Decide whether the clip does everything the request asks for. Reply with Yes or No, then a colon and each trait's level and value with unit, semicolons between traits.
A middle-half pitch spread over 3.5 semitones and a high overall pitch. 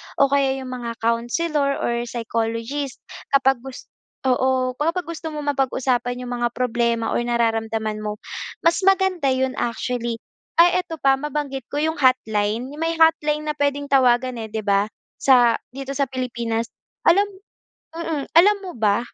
Yes: average, 3.9 semitones; very high, 260 Hz